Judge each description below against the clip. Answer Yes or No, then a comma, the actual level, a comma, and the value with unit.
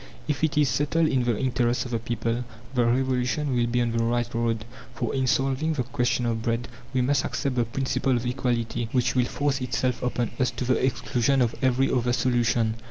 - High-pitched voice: No, low, 125 Hz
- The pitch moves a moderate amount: No, narrow, 1.9 semitones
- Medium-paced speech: No, fast, 210 wpm